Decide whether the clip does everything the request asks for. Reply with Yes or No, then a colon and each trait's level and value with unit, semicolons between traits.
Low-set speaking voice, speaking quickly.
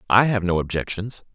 No: low, 100 Hz; average, 180 wpm